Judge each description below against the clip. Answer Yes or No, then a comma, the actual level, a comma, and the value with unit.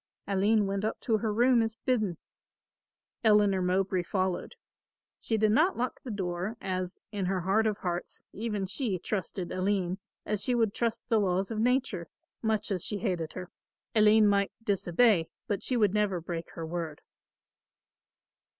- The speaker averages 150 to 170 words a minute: Yes, average, 160 wpm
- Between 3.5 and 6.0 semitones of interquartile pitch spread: No, average, 3.1 semitones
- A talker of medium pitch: No, high, 200 Hz